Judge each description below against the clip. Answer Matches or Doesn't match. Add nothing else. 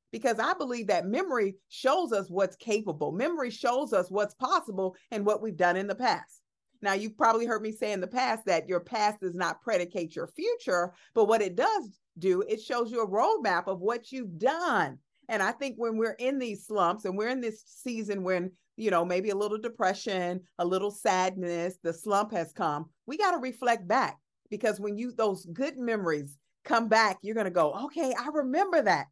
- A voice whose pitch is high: Matches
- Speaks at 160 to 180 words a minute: Doesn't match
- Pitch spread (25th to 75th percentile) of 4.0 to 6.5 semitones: Matches